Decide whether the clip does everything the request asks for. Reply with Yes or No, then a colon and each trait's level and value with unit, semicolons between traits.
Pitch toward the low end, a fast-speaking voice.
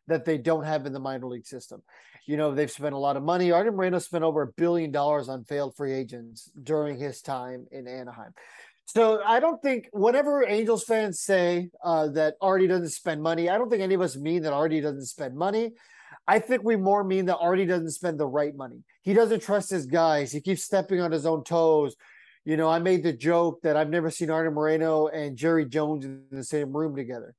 No: medium, 160 Hz; fast, 225 wpm